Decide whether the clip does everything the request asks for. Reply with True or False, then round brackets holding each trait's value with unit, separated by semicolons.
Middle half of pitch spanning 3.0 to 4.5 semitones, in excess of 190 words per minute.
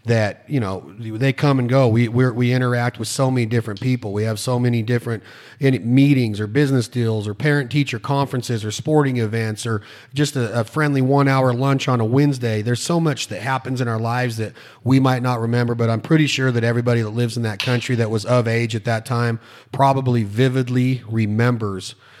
False (2.5 semitones; 205 wpm)